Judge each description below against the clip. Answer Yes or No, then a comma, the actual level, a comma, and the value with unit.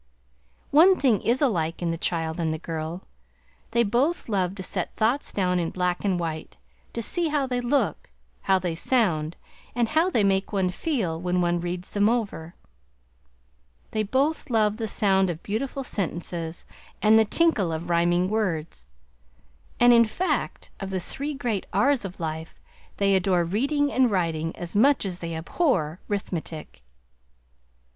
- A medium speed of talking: Yes, average, 160 wpm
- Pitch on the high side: Yes, high, 195 Hz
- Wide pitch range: Yes, wide, 5.7 semitones